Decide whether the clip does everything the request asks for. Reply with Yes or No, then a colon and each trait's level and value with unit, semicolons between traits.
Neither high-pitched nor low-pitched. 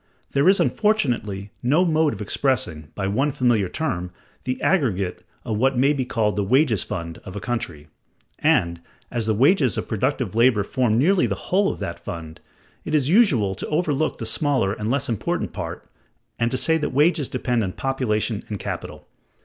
No: low, 120 Hz